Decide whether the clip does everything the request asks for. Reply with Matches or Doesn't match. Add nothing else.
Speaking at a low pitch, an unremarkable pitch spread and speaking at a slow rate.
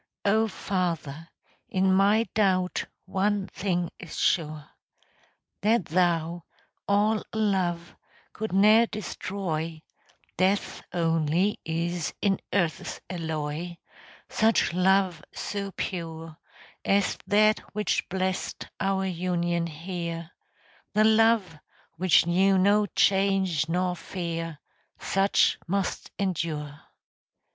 Doesn't match